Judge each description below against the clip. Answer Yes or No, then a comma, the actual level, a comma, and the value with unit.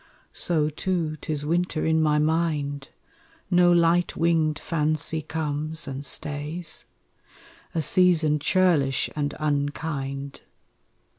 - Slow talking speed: Yes, slow, 100 wpm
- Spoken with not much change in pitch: Yes, narrow, 2.3 semitones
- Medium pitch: Yes, medium, 155 Hz